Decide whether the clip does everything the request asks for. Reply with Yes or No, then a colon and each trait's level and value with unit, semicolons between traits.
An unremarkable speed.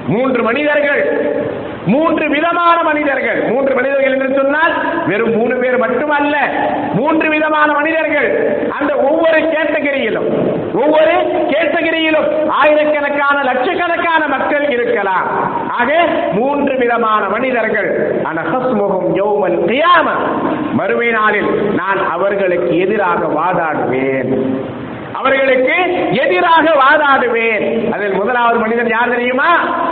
Yes: average, 95 wpm